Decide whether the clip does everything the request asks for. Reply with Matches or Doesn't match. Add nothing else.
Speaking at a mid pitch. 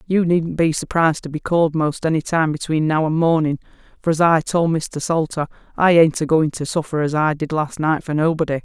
Matches